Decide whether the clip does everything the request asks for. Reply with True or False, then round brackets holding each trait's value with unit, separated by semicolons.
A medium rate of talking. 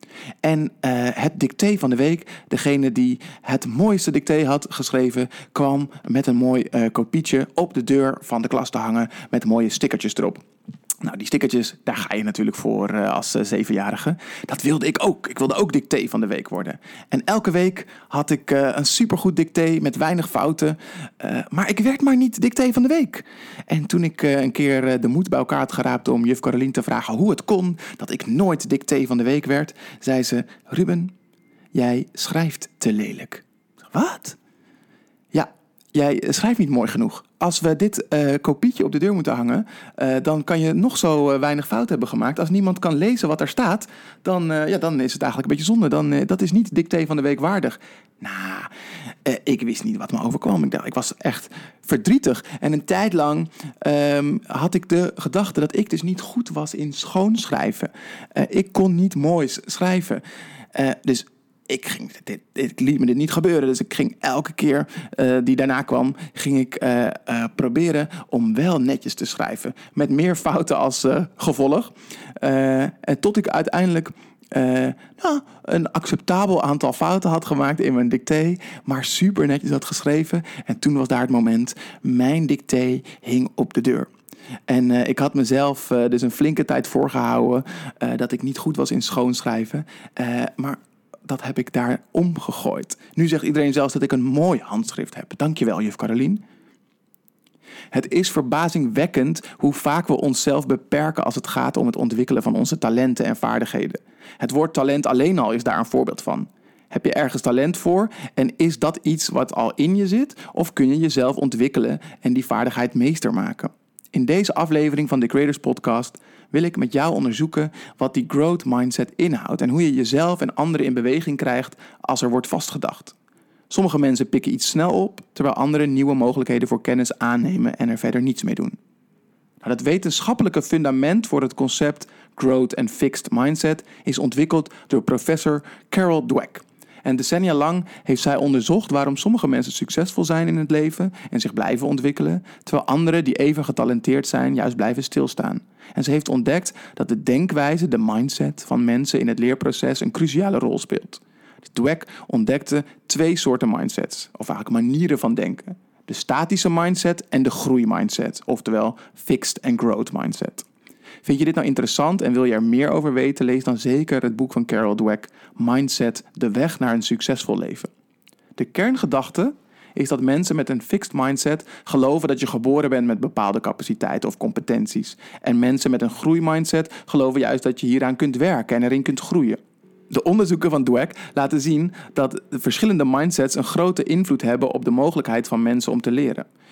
True (190 wpm)